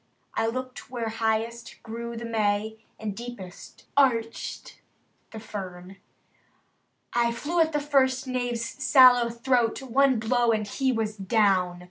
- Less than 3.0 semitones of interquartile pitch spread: Yes, narrow, 2.6 semitones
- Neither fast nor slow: No, slow, 130 wpm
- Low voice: No, high, 235 Hz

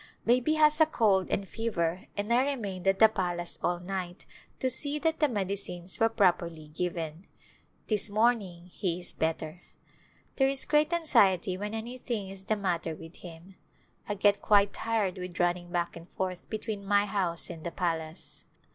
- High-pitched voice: Yes, high, 195 Hz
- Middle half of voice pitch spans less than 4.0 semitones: No, average, 4.3 semitones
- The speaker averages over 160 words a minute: Yes, average, 170 wpm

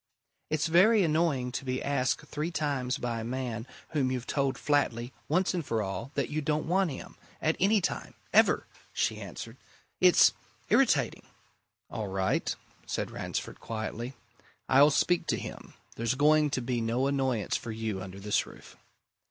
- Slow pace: No, average, 160 wpm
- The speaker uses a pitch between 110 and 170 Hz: Yes, low, 135 Hz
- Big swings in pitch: No, average, 4.5 semitones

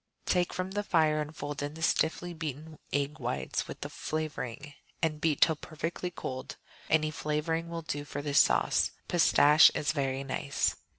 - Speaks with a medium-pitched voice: Yes, medium, 155 Hz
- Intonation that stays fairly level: Yes, narrow, 2.0 semitones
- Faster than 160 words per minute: Yes, average, 170 wpm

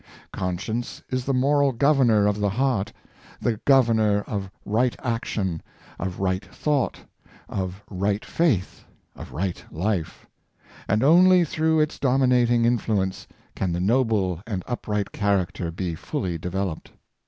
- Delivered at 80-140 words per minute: Yes, slow, 135 wpm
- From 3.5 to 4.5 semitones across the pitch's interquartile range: No, average, 5.1 semitones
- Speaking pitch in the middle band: No, low, 105 Hz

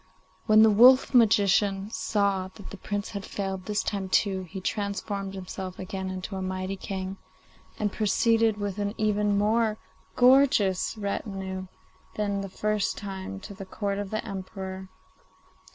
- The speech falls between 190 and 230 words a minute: No, average, 150 wpm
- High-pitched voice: Yes, high, 200 Hz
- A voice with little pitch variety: Yes, narrow, 1.8 semitones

